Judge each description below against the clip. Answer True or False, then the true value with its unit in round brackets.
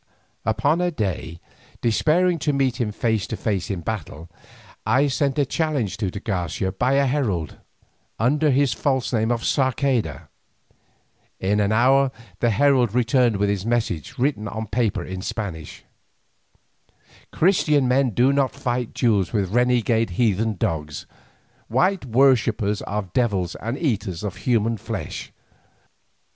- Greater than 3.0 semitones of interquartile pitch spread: True (4.9 semitones)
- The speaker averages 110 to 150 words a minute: True (140 wpm)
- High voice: False (115 Hz)